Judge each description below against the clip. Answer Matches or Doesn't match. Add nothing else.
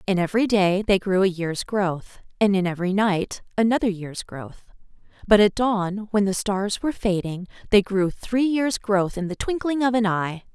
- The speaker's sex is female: Matches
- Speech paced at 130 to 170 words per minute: Doesn't match